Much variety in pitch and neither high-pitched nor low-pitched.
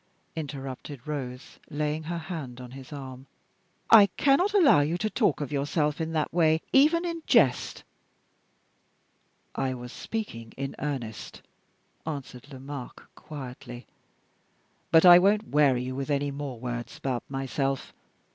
No: average, 3.8 semitones; medium, 145 Hz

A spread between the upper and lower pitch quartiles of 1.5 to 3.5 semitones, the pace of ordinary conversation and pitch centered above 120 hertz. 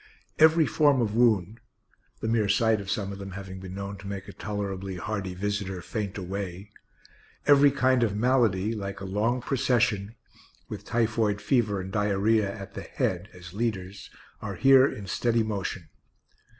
No: average, 3.1 semitones; average, 165 wpm; low, 105 Hz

